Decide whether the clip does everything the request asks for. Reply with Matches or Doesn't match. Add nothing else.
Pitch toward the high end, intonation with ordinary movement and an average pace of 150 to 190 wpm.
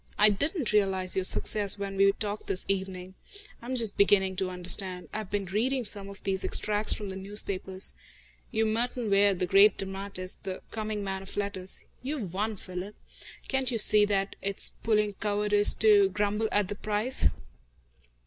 Doesn't match